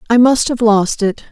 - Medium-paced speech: No, fast, 230 wpm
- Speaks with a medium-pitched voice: No, high, 225 Hz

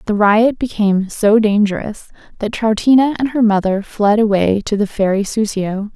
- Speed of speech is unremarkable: Yes, average, 160 wpm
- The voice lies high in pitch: Yes, high, 210 Hz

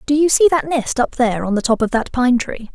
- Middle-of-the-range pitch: No, very high, 255 Hz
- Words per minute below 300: No, fast, 305 wpm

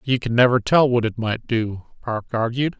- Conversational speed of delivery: No, fast, 215 wpm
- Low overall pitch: Yes, low, 120 Hz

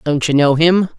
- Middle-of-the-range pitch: Yes, medium, 155 Hz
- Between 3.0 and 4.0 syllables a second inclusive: No, 4.8 syllables/s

